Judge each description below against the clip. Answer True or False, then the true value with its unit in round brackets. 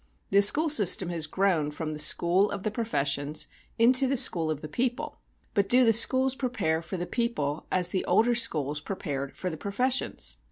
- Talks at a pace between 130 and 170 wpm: False (190 wpm)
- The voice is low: False (195 Hz)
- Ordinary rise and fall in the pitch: False (7.1 semitones)